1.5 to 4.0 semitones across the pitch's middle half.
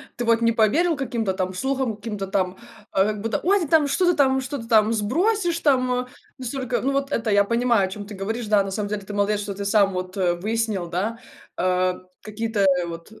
No: average, 4.4 semitones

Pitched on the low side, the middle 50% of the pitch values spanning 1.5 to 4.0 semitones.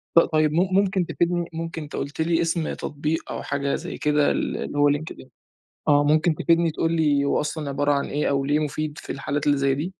No: medium, 150 Hz; narrow, 2.4 semitones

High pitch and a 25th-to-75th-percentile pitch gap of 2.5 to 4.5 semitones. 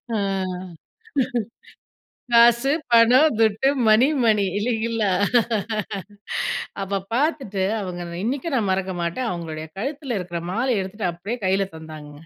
No: high, 210 Hz; average, 4.9 semitones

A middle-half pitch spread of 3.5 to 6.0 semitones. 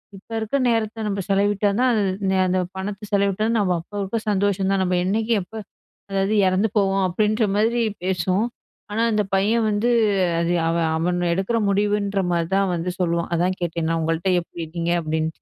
No: average, 2.9 semitones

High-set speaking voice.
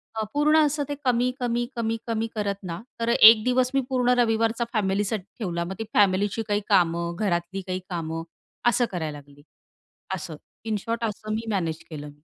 Yes: high, 210 Hz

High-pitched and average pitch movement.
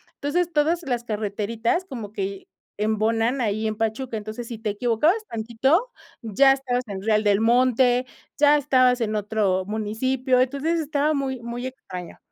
Yes: high, 235 Hz; average, 3.8 semitones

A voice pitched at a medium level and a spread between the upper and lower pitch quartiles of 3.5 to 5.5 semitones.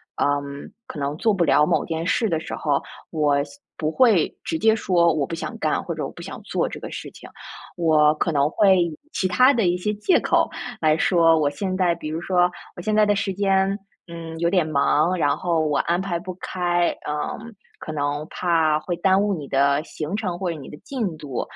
Yes: medium, 170 Hz; average, 3.9 semitones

